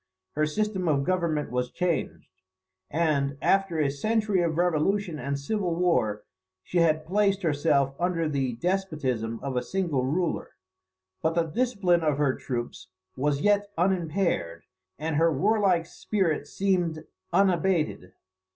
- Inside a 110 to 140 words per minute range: Yes, slow, 135 wpm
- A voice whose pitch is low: No, medium, 165 Hz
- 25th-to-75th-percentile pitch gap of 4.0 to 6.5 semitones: Yes, average, 4.8 semitones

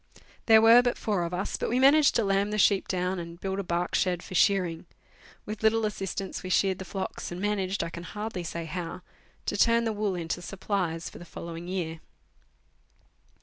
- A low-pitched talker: No, high, 190 Hz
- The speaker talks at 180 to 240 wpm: Yes, fast, 205 wpm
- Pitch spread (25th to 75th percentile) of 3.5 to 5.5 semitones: No, average, 3.1 semitones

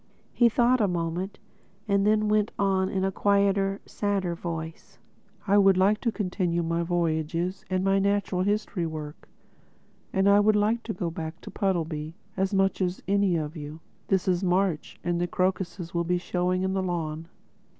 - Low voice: No, medium, 185 Hz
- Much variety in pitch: No, average, 2.7 semitones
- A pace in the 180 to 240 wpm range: No, average, 165 wpm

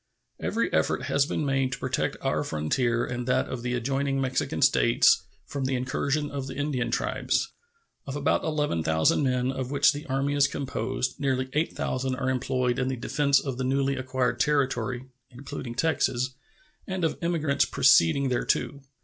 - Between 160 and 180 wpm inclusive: Yes, average, 165 wpm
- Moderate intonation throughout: No, narrow, 1.9 semitones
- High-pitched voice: No, low, 130 Hz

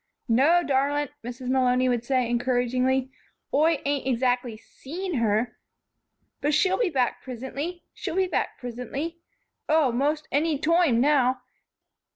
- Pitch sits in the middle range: No, very high, 265 Hz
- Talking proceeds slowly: Yes, slow, 130 wpm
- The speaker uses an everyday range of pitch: Yes, average, 3.7 semitones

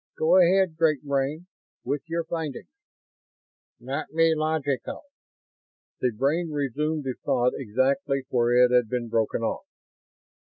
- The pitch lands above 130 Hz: Yes, medium, 140 Hz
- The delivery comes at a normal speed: No, slow, 130 wpm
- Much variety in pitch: No, average, 4.2 semitones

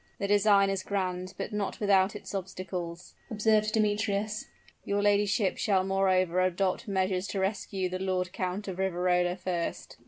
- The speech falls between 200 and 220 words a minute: No, average, 150 wpm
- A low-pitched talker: No, high, 190 Hz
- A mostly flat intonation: Yes, narrow, 1.8 semitones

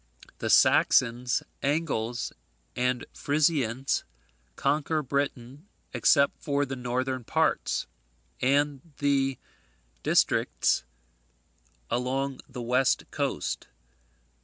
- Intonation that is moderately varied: No, narrow, 2.3 semitones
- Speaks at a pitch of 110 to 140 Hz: Yes, low, 135 Hz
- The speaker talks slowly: Yes, slow, 75 wpm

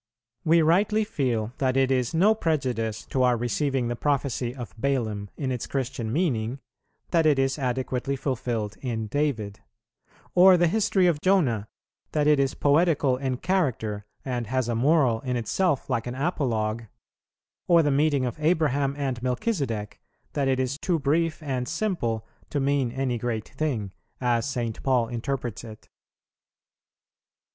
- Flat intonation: No, average, 4.2 semitones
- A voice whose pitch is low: Yes, low, 130 Hz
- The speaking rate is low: No, average, 150 wpm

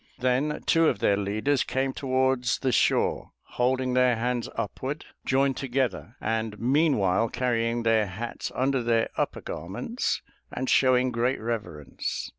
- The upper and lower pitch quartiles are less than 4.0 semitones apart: Yes, average, 2.7 semitones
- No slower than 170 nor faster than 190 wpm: No, slow, 135 wpm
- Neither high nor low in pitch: No, low, 125 Hz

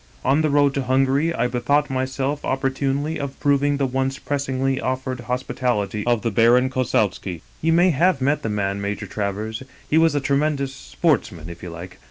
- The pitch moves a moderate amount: Yes, average, 3.9 semitones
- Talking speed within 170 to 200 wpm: Yes, average, 185 wpm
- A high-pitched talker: No, low, 130 Hz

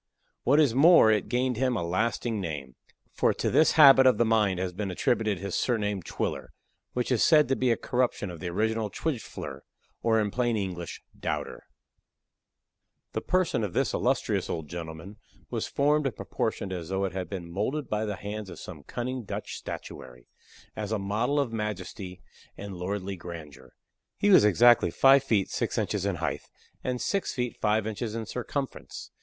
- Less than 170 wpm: No, average, 180 wpm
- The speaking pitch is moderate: No, low, 110 Hz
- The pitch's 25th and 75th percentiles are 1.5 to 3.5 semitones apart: No, average, 4.9 semitones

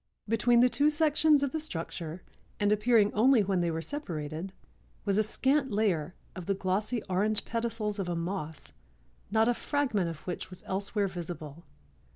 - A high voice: Yes, high, 205 Hz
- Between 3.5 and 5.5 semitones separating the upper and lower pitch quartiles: Yes, average, 5.1 semitones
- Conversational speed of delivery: Yes, average, 170 wpm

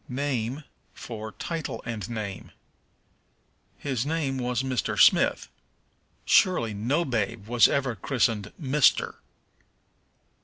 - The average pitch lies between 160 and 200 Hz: No, low, 125 Hz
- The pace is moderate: No, slow, 100 wpm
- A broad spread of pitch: No, average, 4.0 semitones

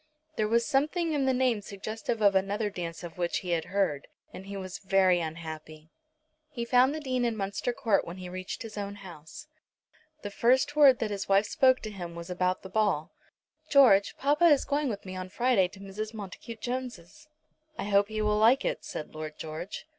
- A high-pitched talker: Yes, high, 205 Hz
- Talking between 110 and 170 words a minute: No, average, 200 wpm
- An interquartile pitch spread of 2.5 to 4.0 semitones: No, average, 5.0 semitones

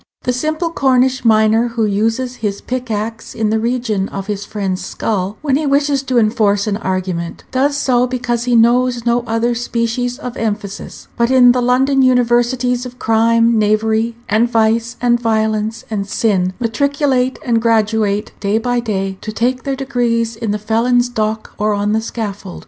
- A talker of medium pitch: No, high, 230 Hz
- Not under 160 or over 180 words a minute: Yes, average, 170 wpm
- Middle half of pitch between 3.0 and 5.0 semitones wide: No, narrow, 2.6 semitones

